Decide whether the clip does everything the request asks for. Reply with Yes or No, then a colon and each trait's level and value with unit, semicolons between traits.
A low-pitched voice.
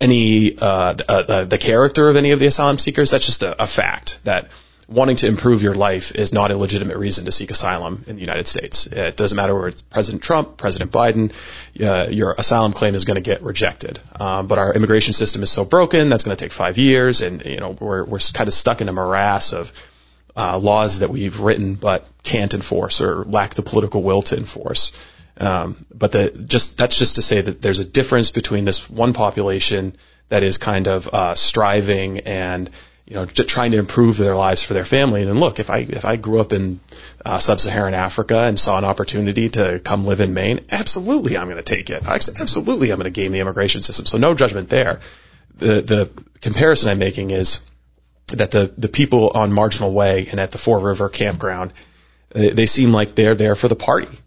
Yes: low, 105 Hz